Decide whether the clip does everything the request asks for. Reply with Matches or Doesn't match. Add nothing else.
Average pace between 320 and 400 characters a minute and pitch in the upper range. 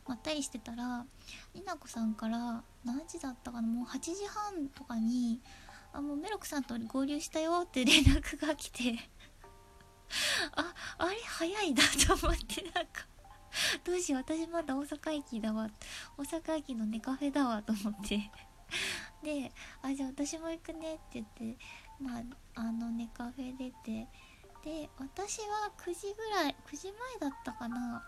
Doesn't match